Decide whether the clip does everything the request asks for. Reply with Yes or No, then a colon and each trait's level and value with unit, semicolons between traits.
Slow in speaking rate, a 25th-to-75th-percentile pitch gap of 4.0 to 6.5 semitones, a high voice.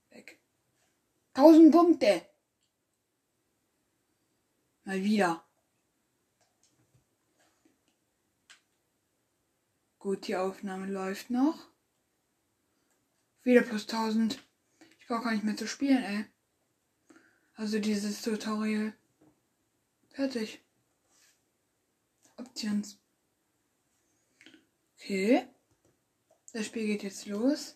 Yes: slow, 65 wpm; average, 4.7 semitones; high, 225 Hz